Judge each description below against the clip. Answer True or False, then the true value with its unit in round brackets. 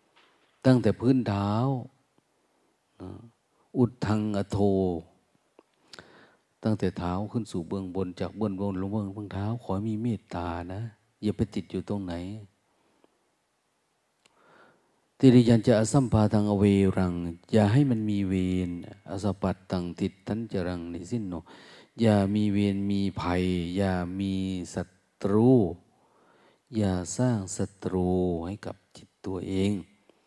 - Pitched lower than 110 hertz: True (100 Hz)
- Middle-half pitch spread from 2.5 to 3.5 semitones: True (2.8 semitones)